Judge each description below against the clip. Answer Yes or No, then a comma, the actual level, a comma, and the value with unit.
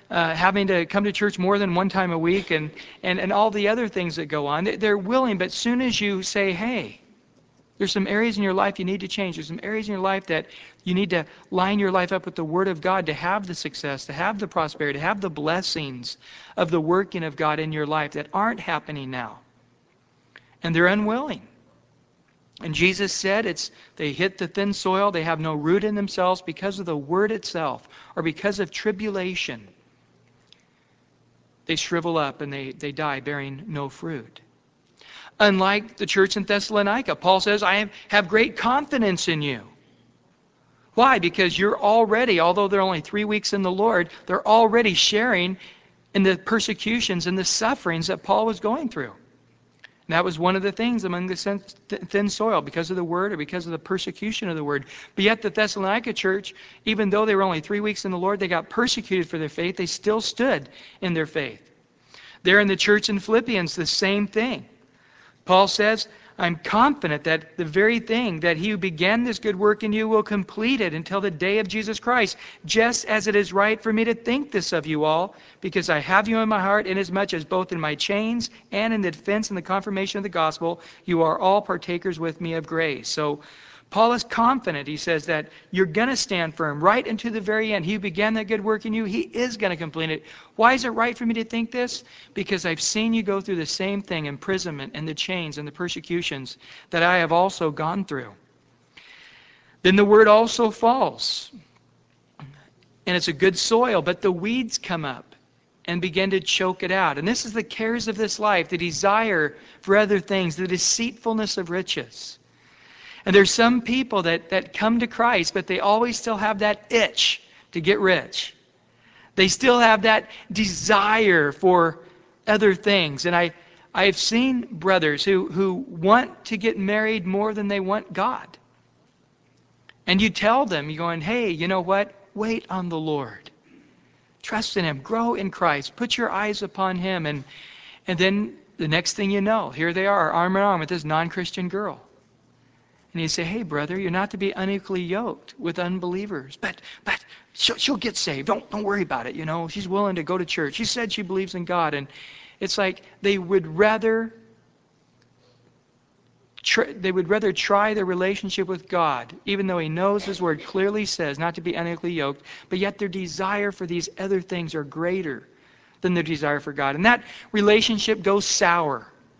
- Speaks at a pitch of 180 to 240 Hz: Yes, high, 190 Hz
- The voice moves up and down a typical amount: Yes, average, 3.8 semitones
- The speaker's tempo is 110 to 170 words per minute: No, average, 200 wpm